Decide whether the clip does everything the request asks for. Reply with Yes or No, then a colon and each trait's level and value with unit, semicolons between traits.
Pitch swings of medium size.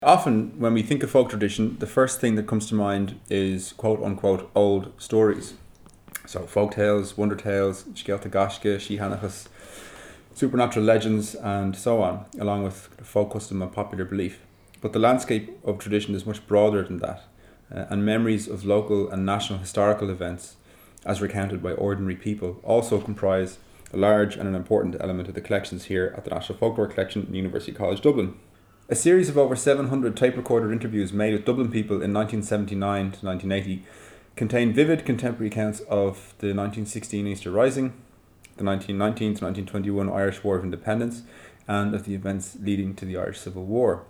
No: narrow, 1.9 semitones